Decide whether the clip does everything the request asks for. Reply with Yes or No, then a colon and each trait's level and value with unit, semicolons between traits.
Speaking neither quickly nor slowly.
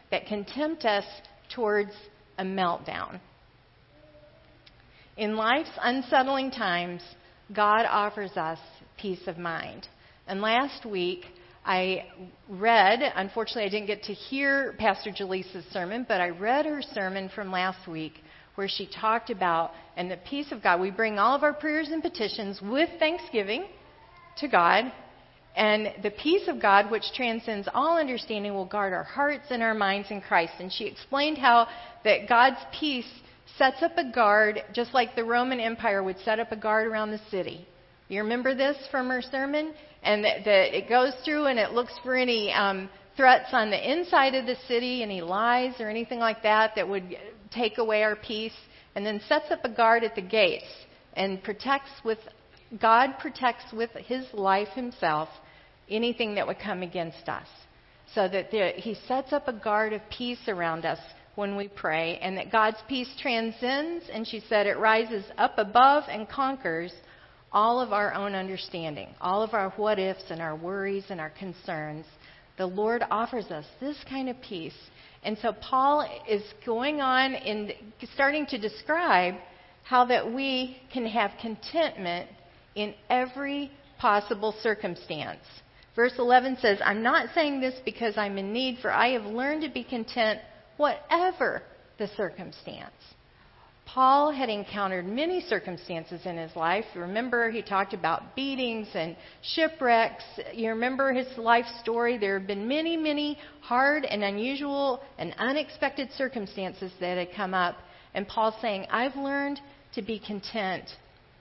Yes: average, 160 wpm